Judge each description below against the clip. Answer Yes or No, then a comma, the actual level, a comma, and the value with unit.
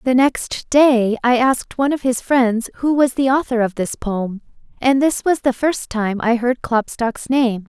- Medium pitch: No, very high, 250 Hz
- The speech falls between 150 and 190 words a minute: No, average, 200 wpm